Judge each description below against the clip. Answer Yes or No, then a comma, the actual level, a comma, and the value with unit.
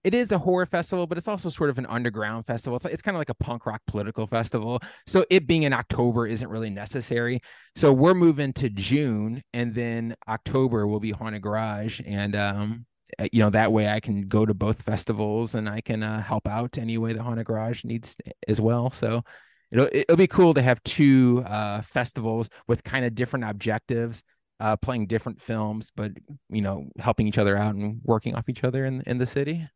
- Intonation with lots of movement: No, average, 3.1 semitones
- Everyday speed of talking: No, fast, 210 wpm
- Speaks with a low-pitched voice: Yes, low, 115 Hz